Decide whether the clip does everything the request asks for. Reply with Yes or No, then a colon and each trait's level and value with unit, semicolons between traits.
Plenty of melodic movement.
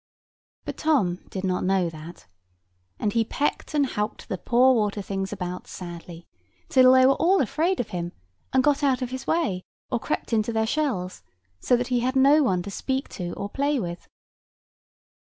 Yes: wide, 6.4 semitones